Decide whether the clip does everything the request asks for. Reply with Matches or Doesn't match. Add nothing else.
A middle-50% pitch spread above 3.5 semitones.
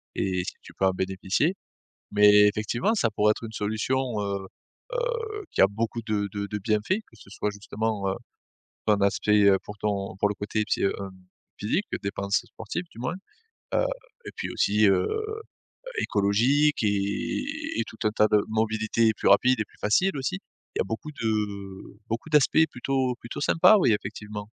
Matches